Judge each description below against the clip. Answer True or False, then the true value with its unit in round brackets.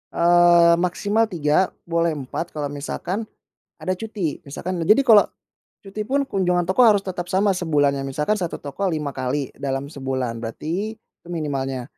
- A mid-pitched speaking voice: True (170 Hz)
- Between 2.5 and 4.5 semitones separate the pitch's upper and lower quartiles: False (5.1 semitones)